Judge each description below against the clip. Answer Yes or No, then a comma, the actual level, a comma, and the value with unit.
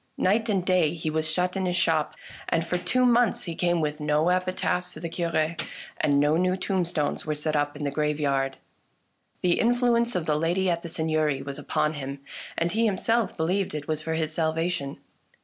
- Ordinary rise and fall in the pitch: Yes, average, 3.3 semitones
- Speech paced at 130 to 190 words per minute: No, average, 200 wpm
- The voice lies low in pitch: No, medium, 165 Hz